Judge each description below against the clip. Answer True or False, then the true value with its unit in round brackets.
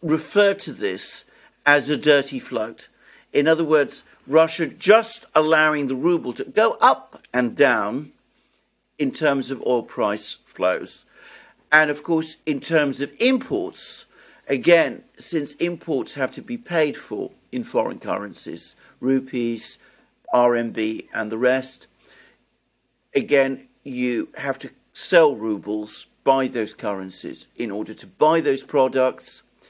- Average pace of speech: False (130 wpm)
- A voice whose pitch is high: False (140 Hz)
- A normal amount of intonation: True (4.4 semitones)